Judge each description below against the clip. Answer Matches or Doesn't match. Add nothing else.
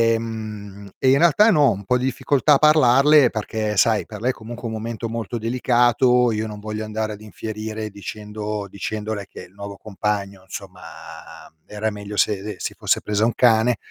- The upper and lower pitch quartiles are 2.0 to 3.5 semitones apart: Matches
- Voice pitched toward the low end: Matches